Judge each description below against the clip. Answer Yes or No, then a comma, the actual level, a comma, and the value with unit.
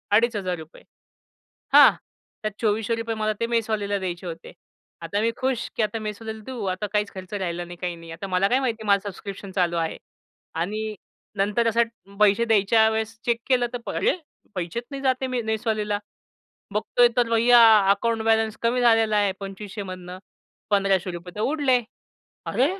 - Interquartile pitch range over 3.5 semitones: No, average, 3.0 semitones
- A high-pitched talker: Yes, high, 215 Hz